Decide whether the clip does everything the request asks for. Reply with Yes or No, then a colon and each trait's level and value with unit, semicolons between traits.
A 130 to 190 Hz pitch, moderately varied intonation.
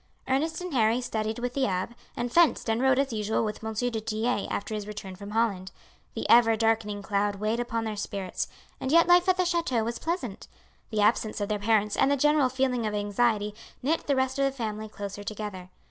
No: high, 225 Hz; average, 3.9 semitones